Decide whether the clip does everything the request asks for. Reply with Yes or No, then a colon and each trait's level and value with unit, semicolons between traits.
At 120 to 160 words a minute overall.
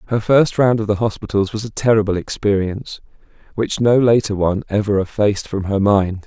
No: average, 180 wpm